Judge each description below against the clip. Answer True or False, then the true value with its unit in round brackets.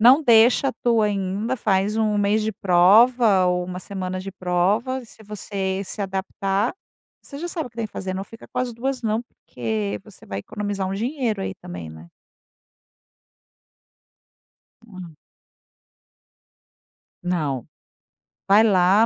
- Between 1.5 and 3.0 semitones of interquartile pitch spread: False (3.5 semitones)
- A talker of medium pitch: False (200 Hz)